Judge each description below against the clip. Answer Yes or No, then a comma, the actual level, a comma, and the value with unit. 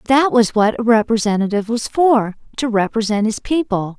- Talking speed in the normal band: Yes, average, 150 wpm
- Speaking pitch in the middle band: No, high, 230 Hz